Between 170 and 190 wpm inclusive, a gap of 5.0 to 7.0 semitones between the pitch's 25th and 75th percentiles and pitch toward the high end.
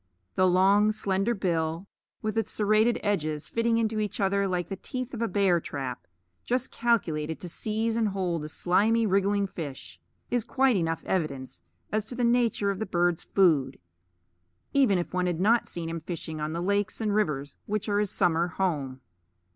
No: average, 180 wpm; average, 4.6 semitones; high, 195 Hz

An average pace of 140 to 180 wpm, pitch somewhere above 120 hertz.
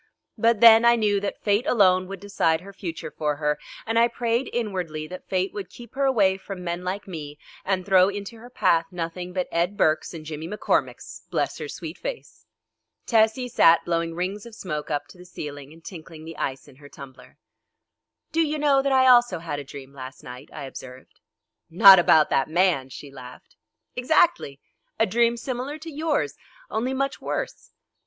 No: average, 190 wpm; medium, 185 Hz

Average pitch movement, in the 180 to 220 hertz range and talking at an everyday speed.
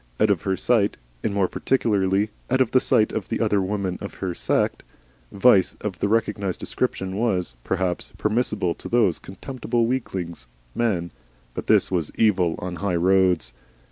No: average, 3.3 semitones; low, 100 Hz; average, 170 wpm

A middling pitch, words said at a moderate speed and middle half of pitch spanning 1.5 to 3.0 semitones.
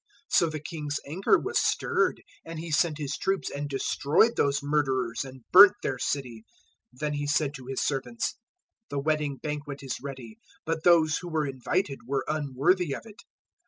Yes: medium, 145 Hz; average, 180 wpm; average, 2.7 semitones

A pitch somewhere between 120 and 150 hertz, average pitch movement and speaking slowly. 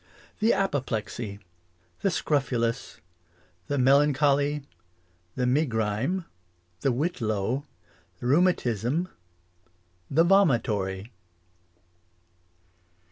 Yes: low, 135 Hz; average, 4.9 semitones; slow, 65 wpm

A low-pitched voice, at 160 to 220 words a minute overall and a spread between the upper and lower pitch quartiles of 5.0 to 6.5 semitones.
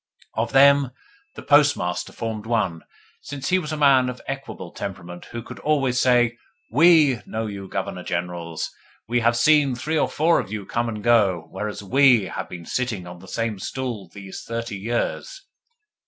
Yes: low, 115 Hz; average, 170 wpm; wide, 5.6 semitones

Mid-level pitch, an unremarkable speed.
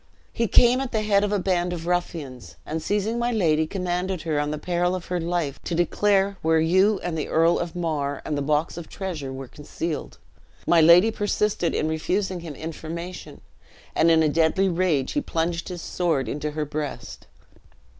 Yes: medium, 170 Hz; average, 190 wpm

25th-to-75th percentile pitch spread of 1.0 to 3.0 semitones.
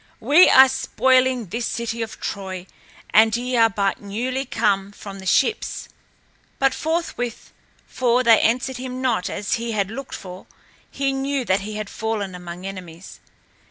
No: average, 4.6 semitones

